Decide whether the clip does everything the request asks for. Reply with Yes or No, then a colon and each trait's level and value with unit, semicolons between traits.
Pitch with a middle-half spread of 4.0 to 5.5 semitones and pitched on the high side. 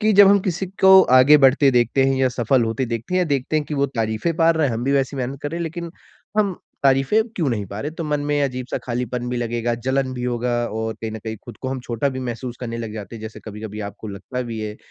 No: average, 4.3 semitones; low, 130 Hz